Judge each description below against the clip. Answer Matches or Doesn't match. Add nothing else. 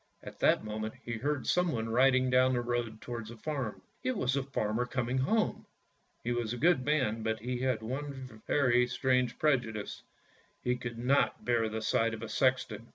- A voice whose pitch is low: Matches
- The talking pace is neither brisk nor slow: Matches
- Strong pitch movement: Doesn't match